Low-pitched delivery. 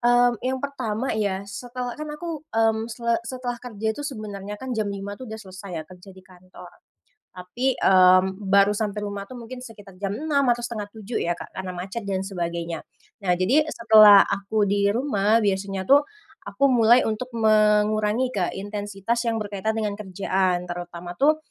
No: high, 210 Hz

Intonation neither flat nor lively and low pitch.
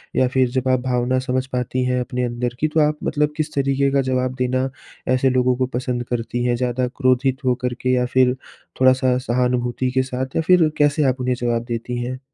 No: narrow, 0.9 semitones; low, 130 Hz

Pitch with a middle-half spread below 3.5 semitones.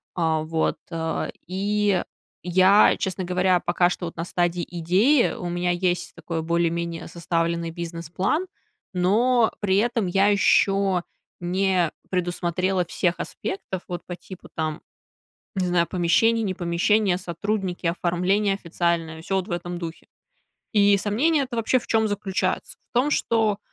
Yes: average, 2.9 semitones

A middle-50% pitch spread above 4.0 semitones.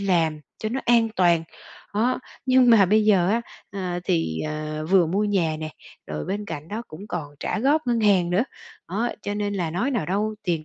Yes: average, 4.7 semitones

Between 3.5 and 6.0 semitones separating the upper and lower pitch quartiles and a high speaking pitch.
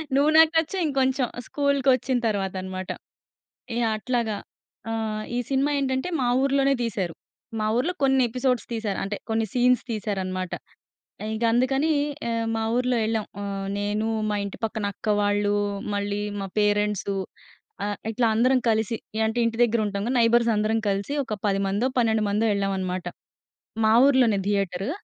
Yes: average, 3.9 semitones; high, 220 Hz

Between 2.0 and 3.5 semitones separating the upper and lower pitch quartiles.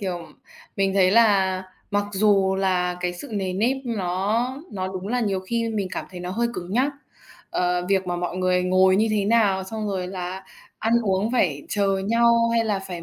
Yes: average, 2.9 semitones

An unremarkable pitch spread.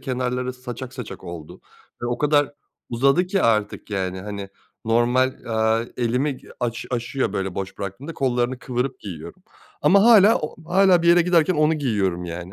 No: wide, 5.7 semitones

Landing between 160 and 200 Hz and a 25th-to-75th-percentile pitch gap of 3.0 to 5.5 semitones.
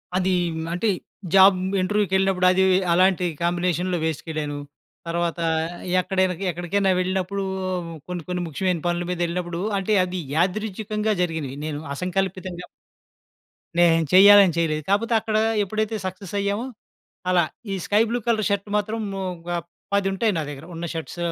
No: medium, 185 Hz; narrow, 2.5 semitones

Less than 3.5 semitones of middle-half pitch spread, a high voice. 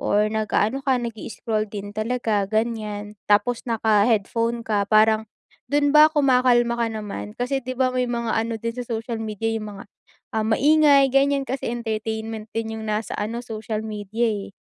Yes: narrow, 2.4 semitones; high, 225 Hz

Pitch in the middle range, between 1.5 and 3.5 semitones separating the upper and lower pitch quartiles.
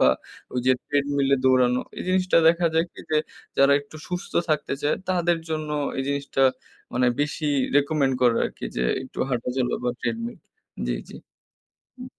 No: medium, 145 Hz; average, 4.0 semitones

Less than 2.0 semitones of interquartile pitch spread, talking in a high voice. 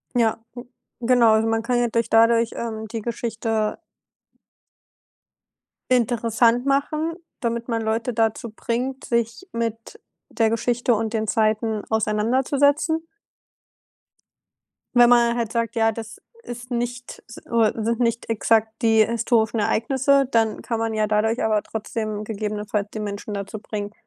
Yes: narrow, 1.6 semitones; high, 230 Hz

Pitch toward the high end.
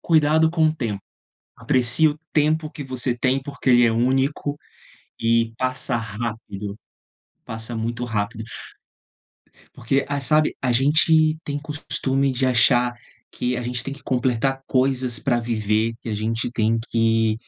No: low, 125 Hz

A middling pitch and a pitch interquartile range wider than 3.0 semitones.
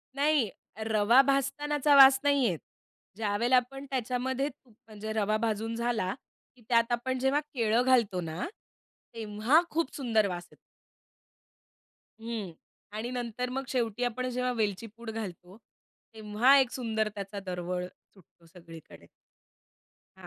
No: high, 230 Hz; average, 3.7 semitones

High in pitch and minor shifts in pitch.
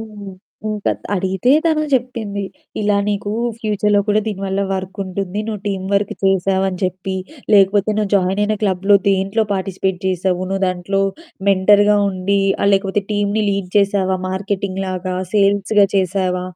Yes: high, 195 Hz; narrow, 1.5 semitones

